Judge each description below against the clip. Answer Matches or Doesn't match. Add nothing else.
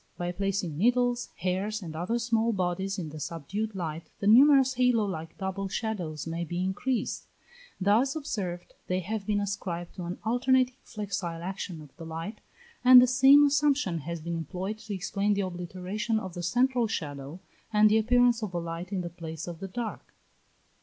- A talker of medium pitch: Doesn't match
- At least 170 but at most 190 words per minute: Matches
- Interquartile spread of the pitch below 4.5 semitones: Doesn't match